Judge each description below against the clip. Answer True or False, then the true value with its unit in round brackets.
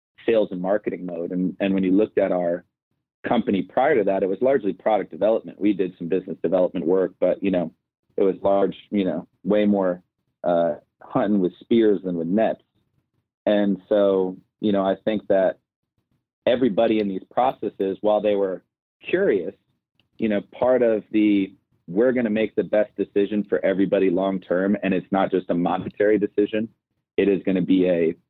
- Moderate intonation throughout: False (2.2 semitones)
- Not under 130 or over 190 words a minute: True (185 wpm)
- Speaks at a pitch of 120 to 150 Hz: False (100 Hz)